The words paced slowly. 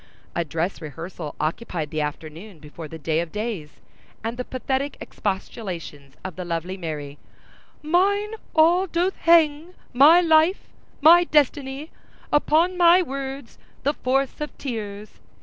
Yes: slow, 125 wpm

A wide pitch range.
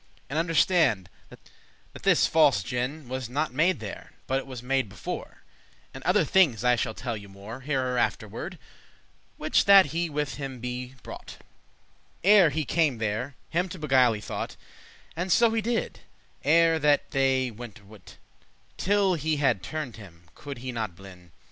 Yes: wide, 6.0 semitones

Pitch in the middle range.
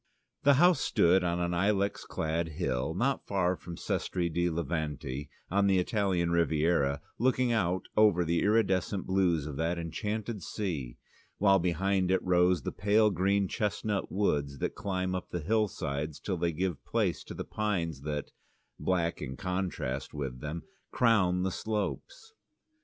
No: very low, 90 Hz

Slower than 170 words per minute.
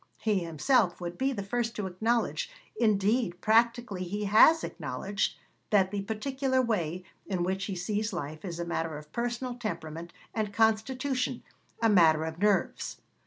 Yes: average, 155 wpm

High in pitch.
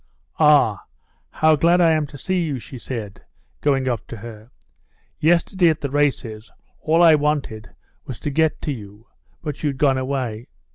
No: medium, 140 Hz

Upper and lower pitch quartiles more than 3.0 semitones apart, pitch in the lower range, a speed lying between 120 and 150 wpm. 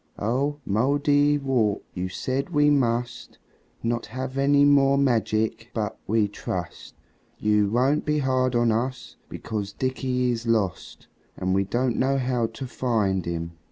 Yes: average, 4.1 semitones; low, 120 Hz; average, 140 wpm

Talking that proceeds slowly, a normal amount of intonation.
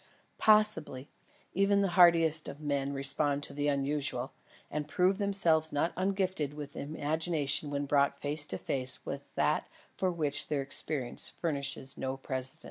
No: average, 145 wpm; average, 3.4 semitones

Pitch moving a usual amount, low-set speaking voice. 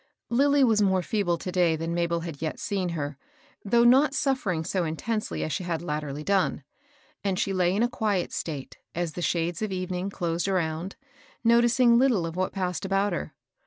No: average, 4.2 semitones; medium, 185 Hz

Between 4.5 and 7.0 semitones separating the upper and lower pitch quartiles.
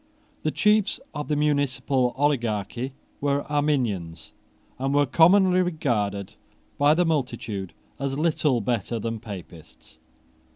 Yes: average, 5.2 semitones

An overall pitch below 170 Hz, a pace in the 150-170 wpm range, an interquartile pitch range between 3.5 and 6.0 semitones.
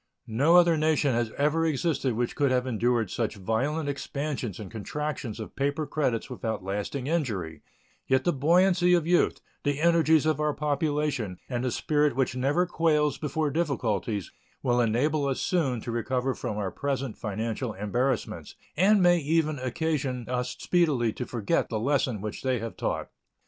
Yes: low, 135 Hz; average, 165 wpm; average, 4.8 semitones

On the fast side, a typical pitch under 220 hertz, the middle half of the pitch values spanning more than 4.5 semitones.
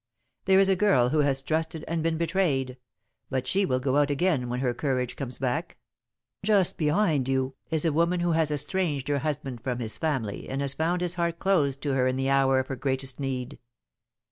No: fast, 210 wpm; medium, 140 Hz; average, 4.2 semitones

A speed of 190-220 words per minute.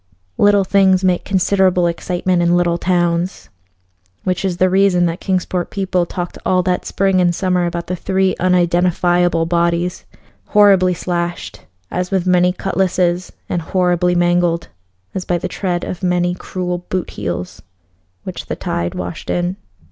No: average, 150 wpm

